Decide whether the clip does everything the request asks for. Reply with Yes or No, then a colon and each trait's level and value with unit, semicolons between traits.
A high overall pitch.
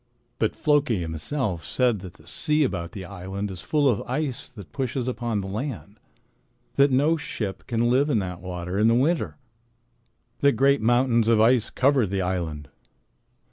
No: low, 115 Hz